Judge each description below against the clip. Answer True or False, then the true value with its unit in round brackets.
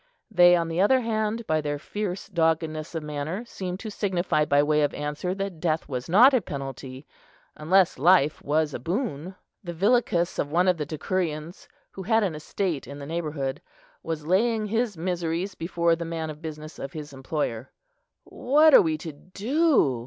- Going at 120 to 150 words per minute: False (180 wpm)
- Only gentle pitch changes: False (4.3 semitones)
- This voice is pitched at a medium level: True (165 Hz)